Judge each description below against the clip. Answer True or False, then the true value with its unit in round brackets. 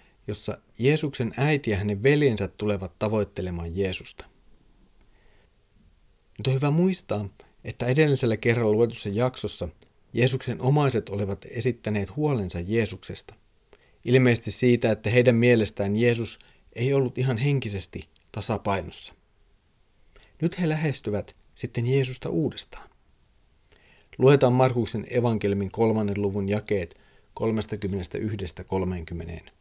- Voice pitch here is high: False (110 Hz)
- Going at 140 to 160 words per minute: False (95 wpm)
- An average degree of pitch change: True (4.1 semitones)